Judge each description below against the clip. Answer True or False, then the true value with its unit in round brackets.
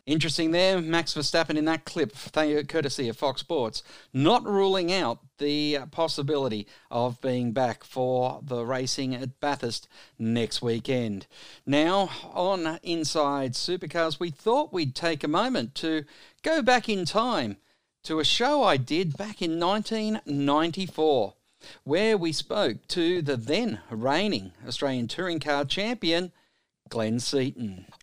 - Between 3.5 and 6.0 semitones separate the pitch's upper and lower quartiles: True (5.0 semitones)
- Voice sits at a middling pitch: True (150 Hz)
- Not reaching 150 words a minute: True (135 wpm)